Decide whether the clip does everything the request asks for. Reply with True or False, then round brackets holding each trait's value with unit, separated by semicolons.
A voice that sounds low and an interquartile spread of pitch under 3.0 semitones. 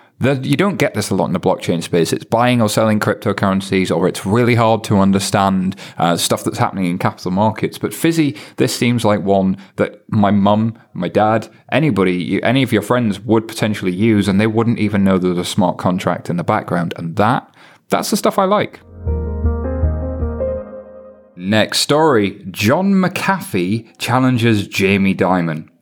False (105 Hz; 3.3 semitones)